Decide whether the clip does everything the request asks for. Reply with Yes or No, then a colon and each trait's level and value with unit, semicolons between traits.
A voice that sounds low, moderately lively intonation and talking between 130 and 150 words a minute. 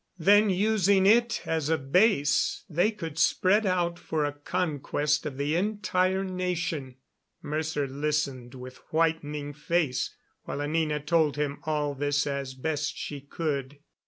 No: medium, 155 Hz; average, 4.0 semitones; slow, 135 wpm